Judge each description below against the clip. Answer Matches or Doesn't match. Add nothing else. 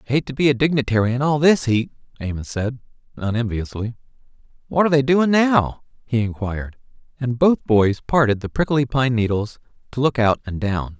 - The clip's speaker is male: Matches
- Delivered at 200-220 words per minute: Doesn't match